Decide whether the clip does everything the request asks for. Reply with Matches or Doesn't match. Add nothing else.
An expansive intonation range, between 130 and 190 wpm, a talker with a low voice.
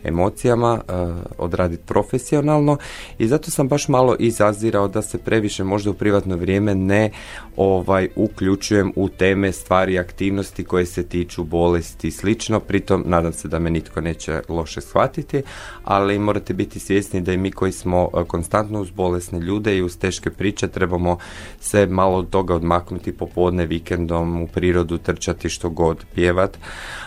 Doesn't match